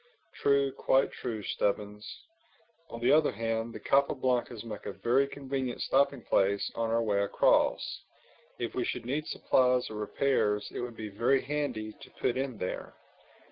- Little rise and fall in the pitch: No, average, 3.9 semitones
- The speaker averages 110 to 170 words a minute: Yes, average, 165 wpm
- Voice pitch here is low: Yes, low, 120 Hz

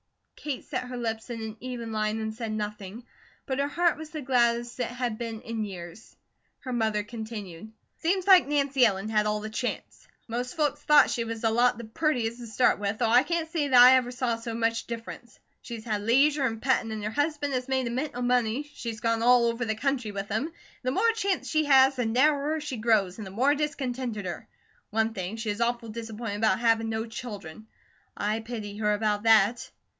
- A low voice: No, high, 235 Hz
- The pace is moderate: No, fast, 215 wpm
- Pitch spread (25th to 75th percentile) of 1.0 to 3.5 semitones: Yes, average, 3.1 semitones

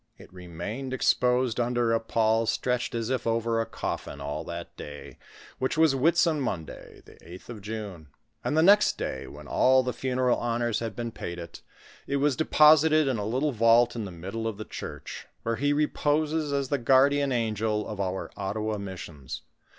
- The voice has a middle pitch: No, low, 115 Hz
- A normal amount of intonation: Yes, average, 4.3 semitones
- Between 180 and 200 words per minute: Yes, average, 185 wpm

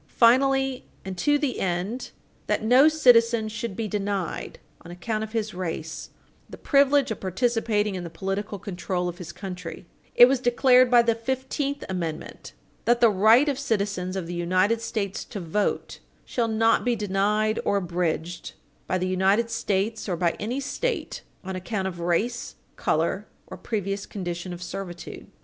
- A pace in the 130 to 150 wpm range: No, average, 165 wpm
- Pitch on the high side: Yes, high, 210 Hz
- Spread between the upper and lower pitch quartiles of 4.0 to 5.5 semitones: Yes, average, 4.5 semitones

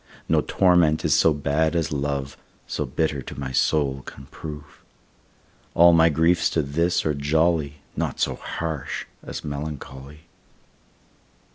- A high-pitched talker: No, very low, 75 Hz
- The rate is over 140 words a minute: No, slow, 135 wpm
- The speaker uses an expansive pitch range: No, narrow, 2.5 semitones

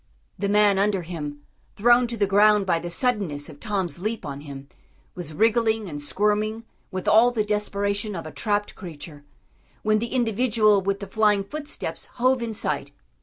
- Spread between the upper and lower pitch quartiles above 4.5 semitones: No, average, 3.7 semitones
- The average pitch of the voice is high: Yes, high, 205 Hz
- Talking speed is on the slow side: No, average, 170 wpm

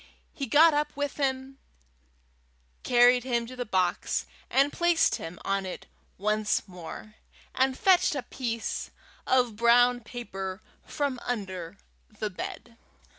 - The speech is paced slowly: Yes, slow, 125 wpm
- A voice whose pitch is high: Yes, high, 240 Hz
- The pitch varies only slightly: No, average, 4.2 semitones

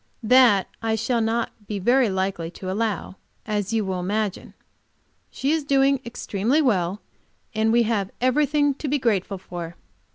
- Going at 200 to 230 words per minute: No, average, 155 wpm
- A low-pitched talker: No, high, 220 Hz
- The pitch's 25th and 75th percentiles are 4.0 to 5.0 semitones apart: Yes, average, 4.7 semitones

